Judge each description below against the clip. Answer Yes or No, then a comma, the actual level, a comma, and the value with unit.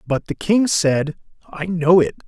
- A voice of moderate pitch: Yes, medium, 170 Hz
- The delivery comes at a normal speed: Yes, average, 185 wpm